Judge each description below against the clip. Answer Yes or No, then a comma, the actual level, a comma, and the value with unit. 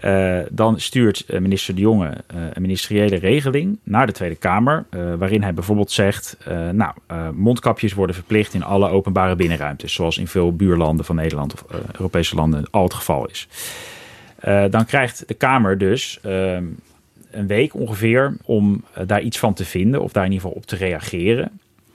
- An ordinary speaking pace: Yes, average, 185 wpm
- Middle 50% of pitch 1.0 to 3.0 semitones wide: No, average, 3.6 semitones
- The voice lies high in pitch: No, very low, 95 Hz